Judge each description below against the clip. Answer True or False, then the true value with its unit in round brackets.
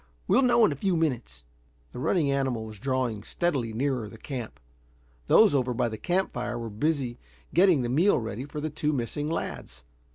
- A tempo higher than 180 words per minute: True (190 wpm)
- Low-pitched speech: True (130 Hz)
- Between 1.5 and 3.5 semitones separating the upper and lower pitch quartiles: False (5.2 semitones)